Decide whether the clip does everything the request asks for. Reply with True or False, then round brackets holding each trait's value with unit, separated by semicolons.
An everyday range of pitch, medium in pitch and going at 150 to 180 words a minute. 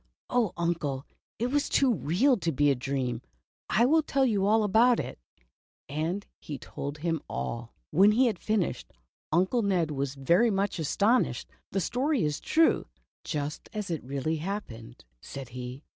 False (7.6 semitones; 170 Hz; 160 wpm)